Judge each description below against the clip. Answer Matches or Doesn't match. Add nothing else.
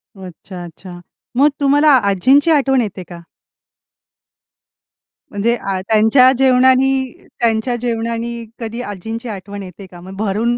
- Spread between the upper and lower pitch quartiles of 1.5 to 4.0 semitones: Doesn't match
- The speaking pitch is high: Matches